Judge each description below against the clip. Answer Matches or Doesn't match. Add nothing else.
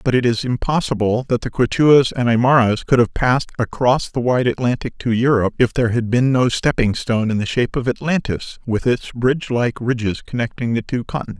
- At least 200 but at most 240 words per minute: Matches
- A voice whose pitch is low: Matches